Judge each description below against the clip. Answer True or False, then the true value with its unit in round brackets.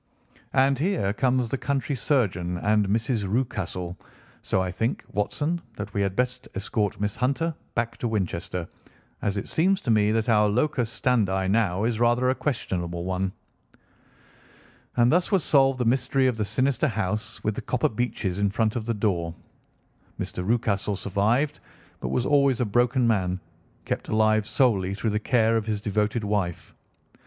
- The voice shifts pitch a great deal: False (4.0 semitones)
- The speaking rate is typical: True (165 wpm)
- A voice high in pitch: False (110 Hz)